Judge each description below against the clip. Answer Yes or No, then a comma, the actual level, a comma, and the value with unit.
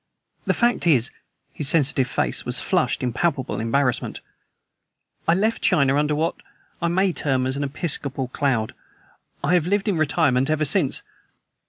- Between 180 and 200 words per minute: No, average, 145 wpm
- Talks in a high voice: No, medium, 145 Hz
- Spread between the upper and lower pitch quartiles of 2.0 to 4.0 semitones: No, average, 4.4 semitones